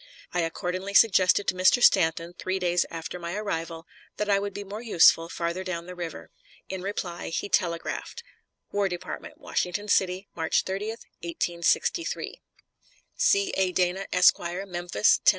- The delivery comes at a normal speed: Yes, average, 150 wpm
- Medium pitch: Yes, medium, 180 Hz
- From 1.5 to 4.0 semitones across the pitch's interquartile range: Yes, narrow, 2.6 semitones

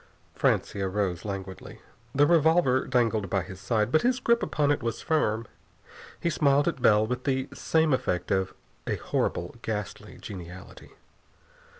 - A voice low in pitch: Yes, low, 115 Hz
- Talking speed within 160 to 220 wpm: No, average, 150 wpm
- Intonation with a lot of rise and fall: Yes, wide, 6.8 semitones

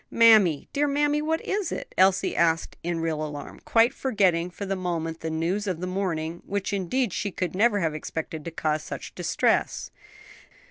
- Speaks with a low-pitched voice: No, medium, 185 Hz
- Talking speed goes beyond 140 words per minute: Yes, average, 180 wpm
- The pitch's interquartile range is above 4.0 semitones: Yes, average, 4.7 semitones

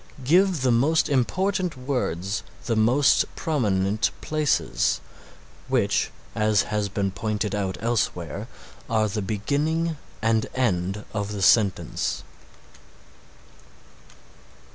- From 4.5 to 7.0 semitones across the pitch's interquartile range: Yes, wide, 5.6 semitones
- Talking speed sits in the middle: No, slow, 100 wpm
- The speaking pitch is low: Yes, low, 110 Hz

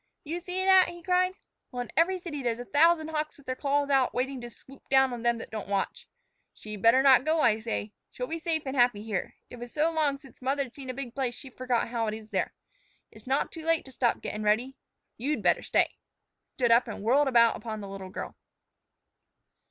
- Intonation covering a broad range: No, average, 4.5 semitones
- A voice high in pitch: Yes, very high, 260 Hz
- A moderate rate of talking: No, fast, 230 wpm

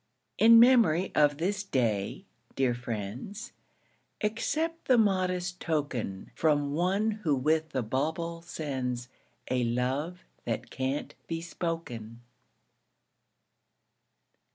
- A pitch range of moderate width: No, wide, 6.6 semitones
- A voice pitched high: No, medium, 155 Hz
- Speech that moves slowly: Yes, slow, 100 wpm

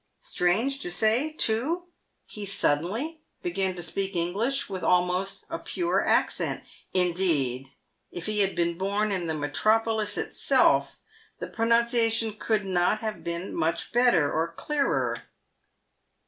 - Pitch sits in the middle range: No, high, 195 Hz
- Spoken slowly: Yes, slow, 130 wpm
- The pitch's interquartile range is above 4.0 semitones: Yes, average, 4.7 semitones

